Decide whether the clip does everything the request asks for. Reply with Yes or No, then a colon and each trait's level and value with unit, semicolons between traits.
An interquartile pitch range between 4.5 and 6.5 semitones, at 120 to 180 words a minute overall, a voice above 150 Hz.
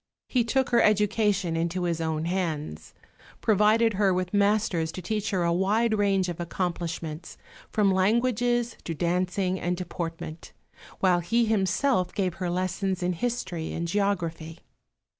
No: average, 3.5 semitones; average, 140 wpm; medium, 185 Hz